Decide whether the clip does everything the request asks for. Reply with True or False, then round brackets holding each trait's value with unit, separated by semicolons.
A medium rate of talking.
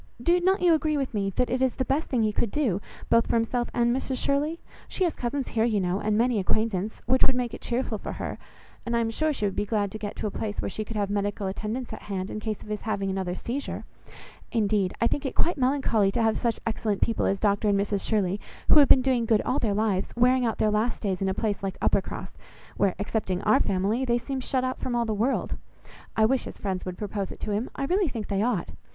False (260 wpm)